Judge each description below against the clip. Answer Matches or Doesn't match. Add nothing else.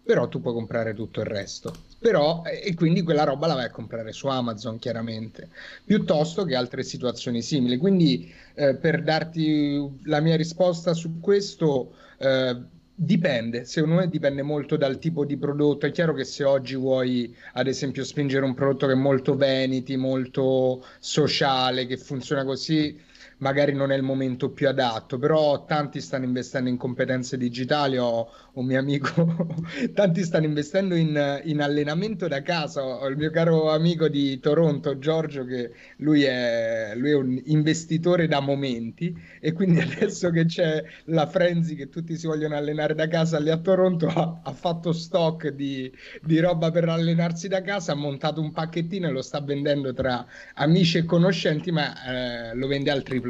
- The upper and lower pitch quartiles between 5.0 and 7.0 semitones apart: Doesn't match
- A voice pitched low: Doesn't match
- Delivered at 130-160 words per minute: Doesn't match